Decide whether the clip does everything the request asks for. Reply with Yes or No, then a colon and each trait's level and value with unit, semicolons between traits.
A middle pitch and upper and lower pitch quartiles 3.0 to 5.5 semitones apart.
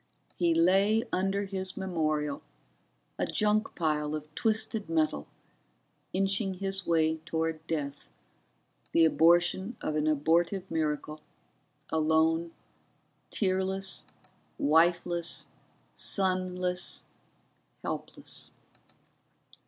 Yes: medium, 170 Hz; average, 3.3 semitones